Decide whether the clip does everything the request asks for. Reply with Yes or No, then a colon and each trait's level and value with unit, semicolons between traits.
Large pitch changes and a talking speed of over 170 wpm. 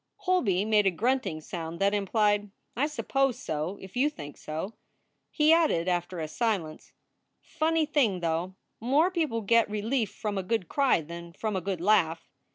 No: wide, 6.9 semitones; average, 165 wpm